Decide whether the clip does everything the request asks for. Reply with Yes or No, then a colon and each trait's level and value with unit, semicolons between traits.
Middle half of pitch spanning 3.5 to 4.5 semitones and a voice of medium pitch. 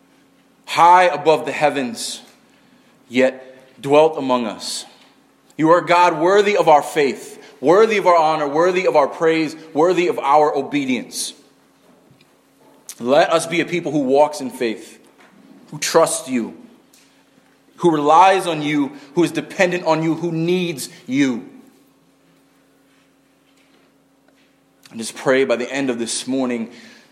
Yes: average, 4.0 semitones; medium, 160 Hz